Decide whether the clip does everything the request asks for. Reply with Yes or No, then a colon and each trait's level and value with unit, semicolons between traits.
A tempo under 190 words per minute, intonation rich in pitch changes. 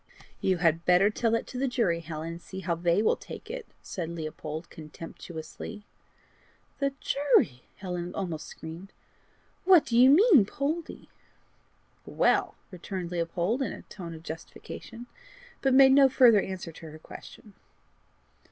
Yes: average, 145 wpm; wide, 6.9 semitones